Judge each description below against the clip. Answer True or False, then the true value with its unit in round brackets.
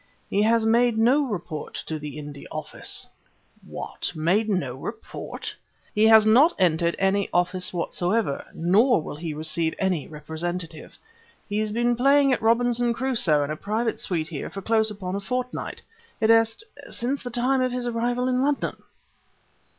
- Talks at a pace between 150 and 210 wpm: True (160 wpm)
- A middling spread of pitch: False (6.2 semitones)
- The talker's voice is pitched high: True (215 Hz)